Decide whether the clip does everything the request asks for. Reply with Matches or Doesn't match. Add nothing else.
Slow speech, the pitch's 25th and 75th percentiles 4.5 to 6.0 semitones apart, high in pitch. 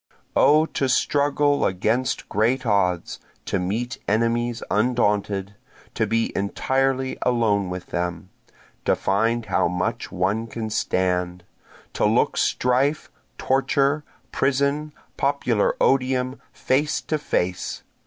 Doesn't match